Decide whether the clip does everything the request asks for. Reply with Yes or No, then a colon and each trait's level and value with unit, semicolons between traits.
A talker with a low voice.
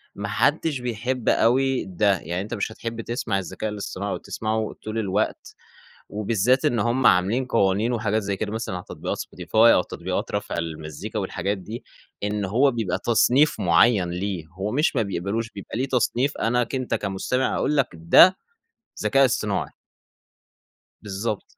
Yes: low, 110 Hz